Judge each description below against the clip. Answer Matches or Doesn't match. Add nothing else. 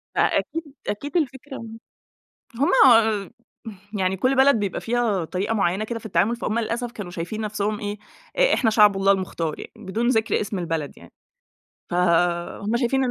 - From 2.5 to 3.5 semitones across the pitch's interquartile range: Doesn't match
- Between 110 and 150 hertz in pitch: Doesn't match